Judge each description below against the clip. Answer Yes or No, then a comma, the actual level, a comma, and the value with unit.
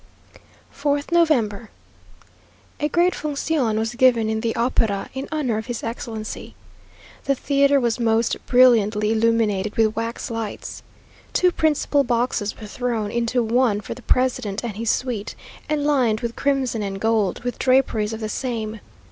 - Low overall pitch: No, high, 235 Hz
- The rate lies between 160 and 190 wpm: No, average, 150 wpm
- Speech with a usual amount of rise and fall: Yes, average, 3.1 semitones